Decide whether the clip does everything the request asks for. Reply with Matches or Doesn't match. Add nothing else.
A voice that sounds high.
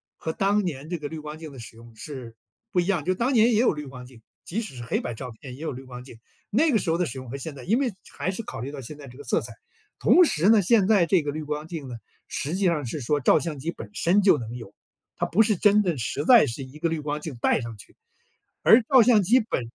Doesn't match